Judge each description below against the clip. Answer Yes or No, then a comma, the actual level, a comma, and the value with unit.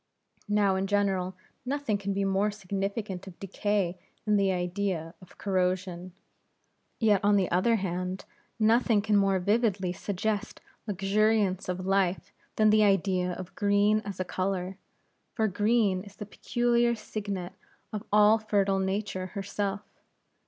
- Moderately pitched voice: No, high, 200 Hz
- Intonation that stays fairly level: Yes, narrow, 2.1 semitones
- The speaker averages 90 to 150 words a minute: Yes, average, 140 wpm